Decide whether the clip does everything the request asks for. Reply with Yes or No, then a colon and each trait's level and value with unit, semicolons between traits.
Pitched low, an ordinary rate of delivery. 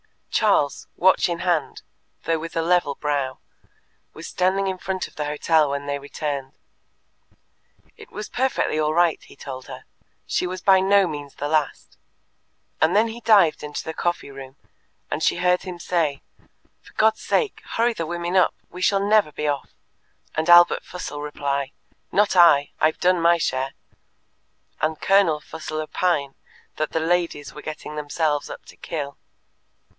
No: medium, 165 Hz; average, 165 wpm